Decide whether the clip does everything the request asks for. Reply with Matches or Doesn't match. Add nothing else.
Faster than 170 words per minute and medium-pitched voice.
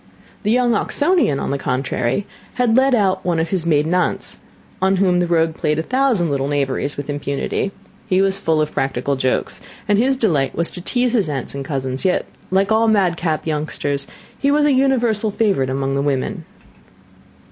Matches